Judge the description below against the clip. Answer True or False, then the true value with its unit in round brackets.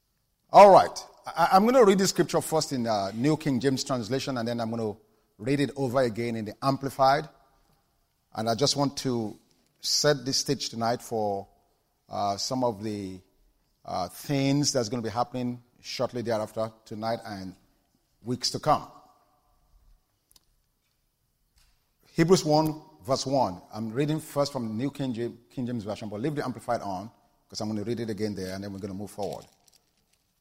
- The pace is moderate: True (175 wpm)